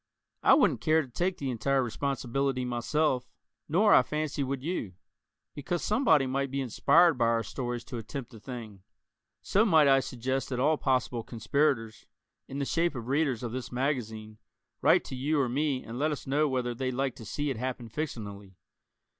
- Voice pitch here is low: Yes, low, 130 Hz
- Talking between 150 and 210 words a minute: Yes, average, 185 wpm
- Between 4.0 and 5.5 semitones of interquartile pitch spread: No, average, 3.4 semitones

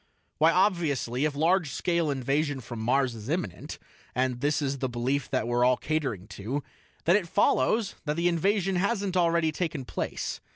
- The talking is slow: No, average, 170 wpm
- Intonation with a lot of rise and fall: No, average, 5.0 semitones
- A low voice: No, medium, 145 Hz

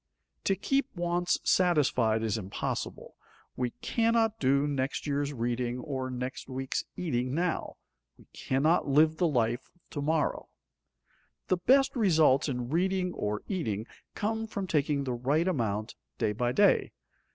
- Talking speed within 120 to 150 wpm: Yes, average, 140 wpm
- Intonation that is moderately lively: No, wide, 6.2 semitones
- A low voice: No, medium, 145 Hz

